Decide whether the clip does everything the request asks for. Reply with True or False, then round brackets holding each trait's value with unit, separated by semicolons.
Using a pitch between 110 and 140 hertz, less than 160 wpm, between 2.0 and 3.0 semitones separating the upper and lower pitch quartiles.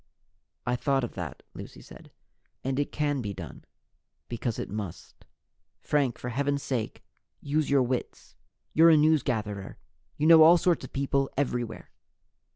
False (135 Hz; 150 wpm; 3.7 semitones)